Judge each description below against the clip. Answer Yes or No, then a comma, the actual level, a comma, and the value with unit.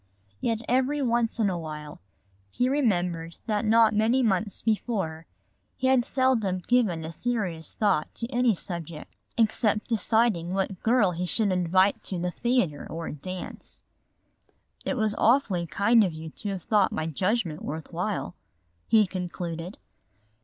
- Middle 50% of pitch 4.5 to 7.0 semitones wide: Yes, average, 5.2 semitones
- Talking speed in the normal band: Yes, average, 150 wpm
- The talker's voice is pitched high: Yes, high, 200 Hz